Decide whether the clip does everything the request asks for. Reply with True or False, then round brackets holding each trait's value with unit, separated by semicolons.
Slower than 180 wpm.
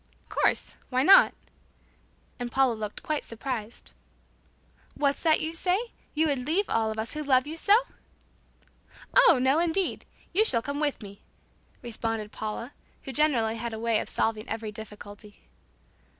True (160 wpm)